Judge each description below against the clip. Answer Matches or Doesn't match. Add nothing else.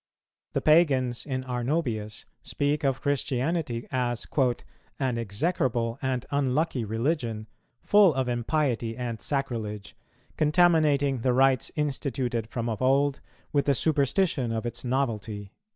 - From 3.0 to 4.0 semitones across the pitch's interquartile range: Matches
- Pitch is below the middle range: Matches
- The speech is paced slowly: Matches